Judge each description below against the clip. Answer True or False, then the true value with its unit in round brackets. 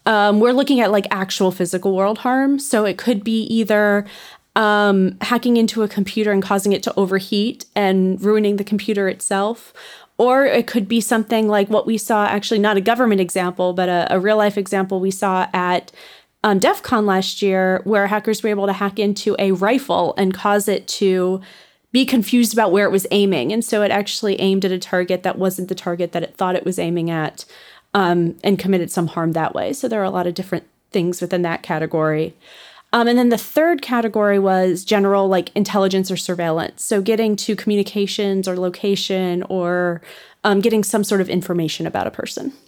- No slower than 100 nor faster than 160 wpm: False (200 wpm)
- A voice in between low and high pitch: False (200 Hz)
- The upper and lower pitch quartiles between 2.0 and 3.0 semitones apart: True (2.7 semitones)